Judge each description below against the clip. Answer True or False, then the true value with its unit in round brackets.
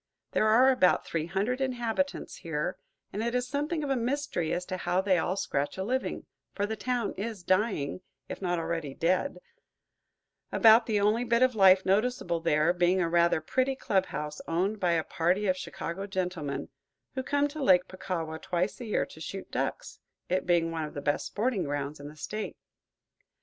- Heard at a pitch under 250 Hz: True (190 Hz)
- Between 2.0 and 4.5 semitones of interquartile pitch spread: False (5.6 semitones)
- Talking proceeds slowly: False (190 wpm)